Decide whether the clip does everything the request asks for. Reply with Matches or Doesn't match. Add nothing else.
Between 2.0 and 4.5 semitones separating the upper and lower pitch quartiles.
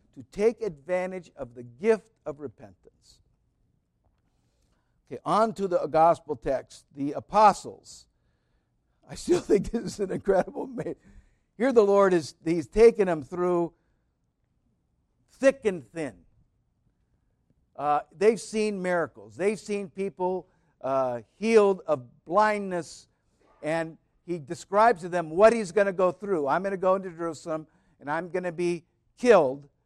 Doesn't match